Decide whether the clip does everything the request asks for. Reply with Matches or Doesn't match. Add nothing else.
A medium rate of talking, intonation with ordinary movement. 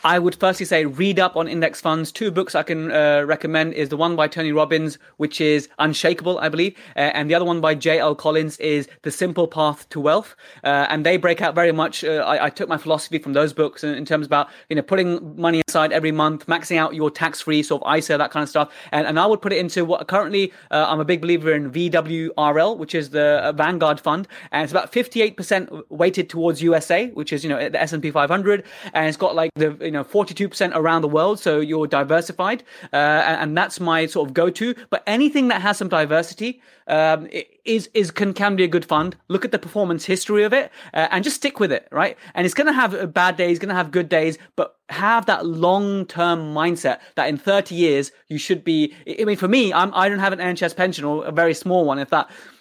Doesn't match